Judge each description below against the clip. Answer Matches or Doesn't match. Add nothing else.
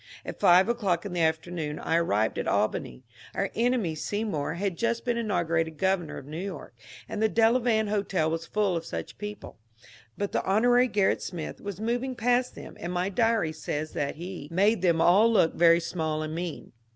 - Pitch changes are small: Doesn't match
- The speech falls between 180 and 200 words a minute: Matches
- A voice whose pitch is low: Doesn't match